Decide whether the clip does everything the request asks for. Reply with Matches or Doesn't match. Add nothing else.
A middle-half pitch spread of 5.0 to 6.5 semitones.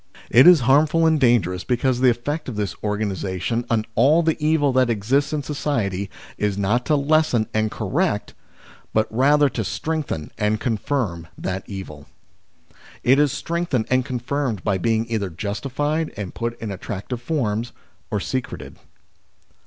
Matches